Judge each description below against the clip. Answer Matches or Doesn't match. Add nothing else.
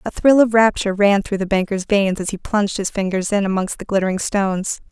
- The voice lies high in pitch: Matches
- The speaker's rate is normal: Doesn't match